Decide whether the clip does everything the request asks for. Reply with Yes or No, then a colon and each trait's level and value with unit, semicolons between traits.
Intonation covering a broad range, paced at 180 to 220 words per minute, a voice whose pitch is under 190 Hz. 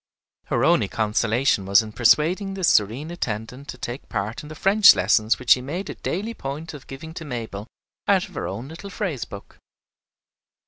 Yes: wide, 7.4 semitones; average, 190 wpm; low, 135 Hz